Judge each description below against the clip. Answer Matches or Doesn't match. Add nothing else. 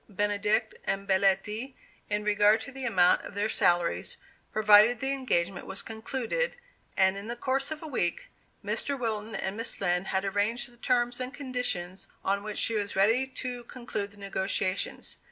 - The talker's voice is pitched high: Matches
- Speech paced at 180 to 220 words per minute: Doesn't match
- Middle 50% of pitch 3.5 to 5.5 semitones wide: Matches